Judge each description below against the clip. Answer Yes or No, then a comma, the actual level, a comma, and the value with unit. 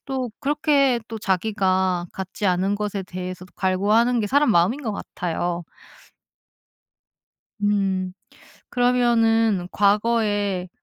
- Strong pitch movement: No, average, 3.9 semitones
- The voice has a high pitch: Yes, high, 205 Hz